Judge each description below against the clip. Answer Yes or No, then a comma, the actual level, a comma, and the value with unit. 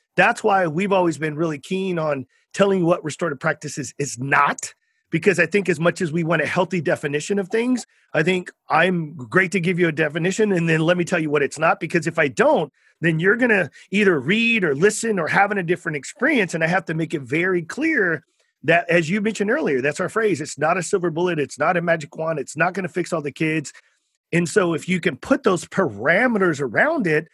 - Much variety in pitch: No, average, 3.5 semitones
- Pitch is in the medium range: Yes, medium, 175 Hz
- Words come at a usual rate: No, fast, 235 wpm